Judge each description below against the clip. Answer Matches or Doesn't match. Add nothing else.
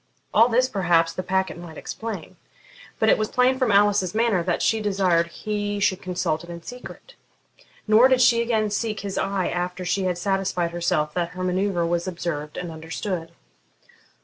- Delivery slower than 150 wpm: Doesn't match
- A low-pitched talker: Doesn't match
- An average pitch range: Matches